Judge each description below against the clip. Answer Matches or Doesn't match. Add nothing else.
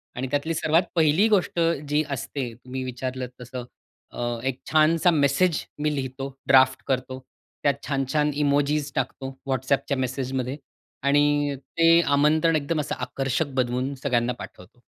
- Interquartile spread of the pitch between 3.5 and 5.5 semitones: Doesn't match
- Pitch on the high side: Doesn't match